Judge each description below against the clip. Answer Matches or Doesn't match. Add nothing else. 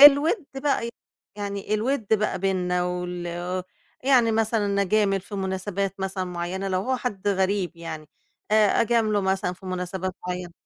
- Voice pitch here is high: Matches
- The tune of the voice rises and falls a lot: Doesn't match